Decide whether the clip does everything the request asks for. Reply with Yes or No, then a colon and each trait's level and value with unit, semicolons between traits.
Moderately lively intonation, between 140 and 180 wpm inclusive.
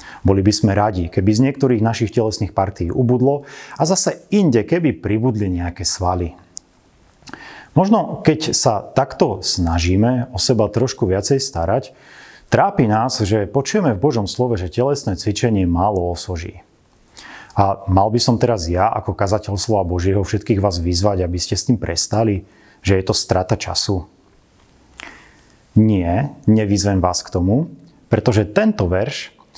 Yes: average, 4.9 semitones; average, 145 wpm